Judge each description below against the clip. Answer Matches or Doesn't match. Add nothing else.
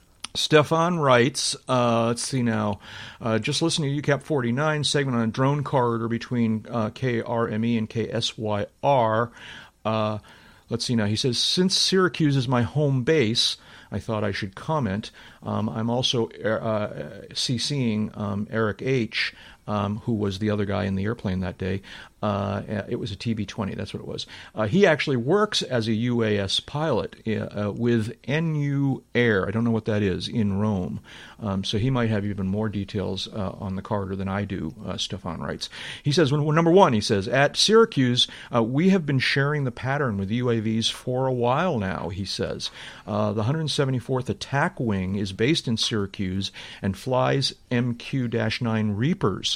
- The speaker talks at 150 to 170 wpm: Doesn't match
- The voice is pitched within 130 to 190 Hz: Doesn't match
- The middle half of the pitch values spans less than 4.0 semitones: Doesn't match